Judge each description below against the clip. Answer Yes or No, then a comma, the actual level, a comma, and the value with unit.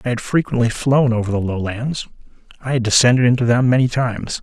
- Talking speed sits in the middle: Yes, average, 190 wpm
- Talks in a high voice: No, low, 120 Hz